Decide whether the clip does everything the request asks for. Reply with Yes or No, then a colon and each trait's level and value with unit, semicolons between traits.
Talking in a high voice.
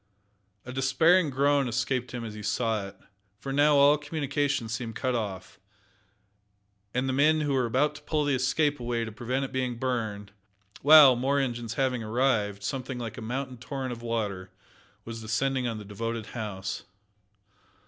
No: low, 125 Hz